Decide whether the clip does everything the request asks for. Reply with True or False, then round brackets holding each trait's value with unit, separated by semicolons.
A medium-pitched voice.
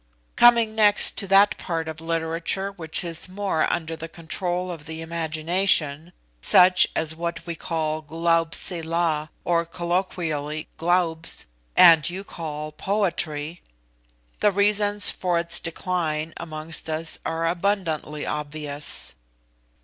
True (165 Hz)